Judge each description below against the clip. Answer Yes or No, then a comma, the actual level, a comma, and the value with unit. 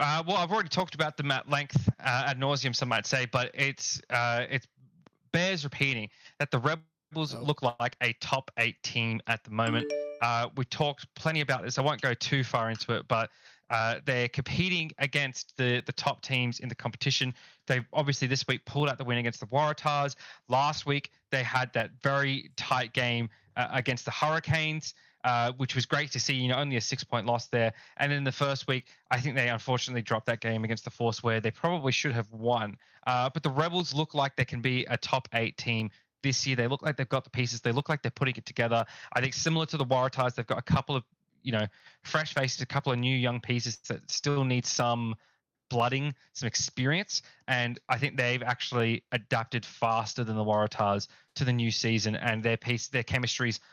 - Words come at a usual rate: No, fast, 215 wpm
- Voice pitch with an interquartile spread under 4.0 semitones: Yes, average, 3.1 semitones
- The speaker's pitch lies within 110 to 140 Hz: Yes, low, 130 Hz